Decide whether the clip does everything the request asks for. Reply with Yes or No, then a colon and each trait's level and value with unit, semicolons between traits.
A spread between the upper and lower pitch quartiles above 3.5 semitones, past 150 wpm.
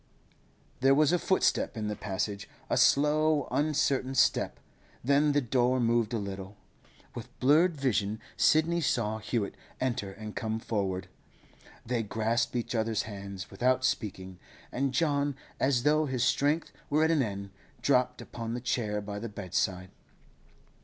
No: average, 5.2 semitones; average, 145 wpm